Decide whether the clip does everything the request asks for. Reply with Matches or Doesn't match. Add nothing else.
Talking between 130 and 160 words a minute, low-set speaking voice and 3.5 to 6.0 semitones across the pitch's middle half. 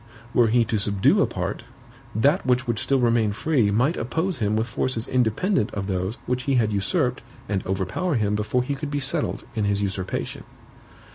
Doesn't match